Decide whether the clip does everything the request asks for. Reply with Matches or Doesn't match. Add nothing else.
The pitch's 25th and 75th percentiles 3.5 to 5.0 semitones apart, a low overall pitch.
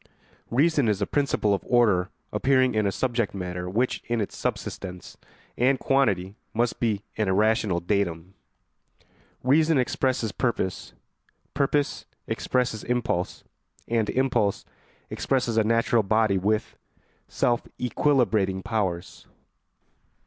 Matches